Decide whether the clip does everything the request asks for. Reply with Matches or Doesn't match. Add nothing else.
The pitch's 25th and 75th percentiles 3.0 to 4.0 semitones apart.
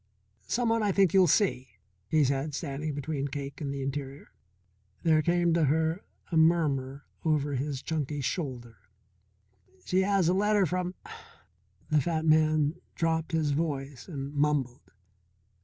Matches